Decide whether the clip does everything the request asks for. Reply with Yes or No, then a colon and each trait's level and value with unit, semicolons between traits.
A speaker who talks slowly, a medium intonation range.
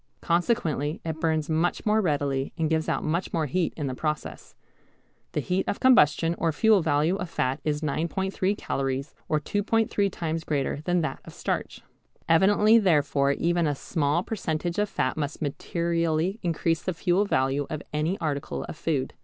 No: average, 170 wpm; average, 3.6 semitones